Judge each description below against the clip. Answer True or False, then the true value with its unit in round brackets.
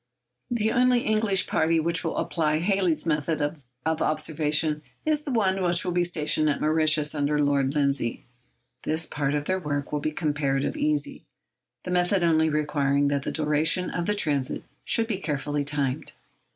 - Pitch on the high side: False (155 Hz)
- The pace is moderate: True (165 wpm)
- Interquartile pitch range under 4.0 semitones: True (3.6 semitones)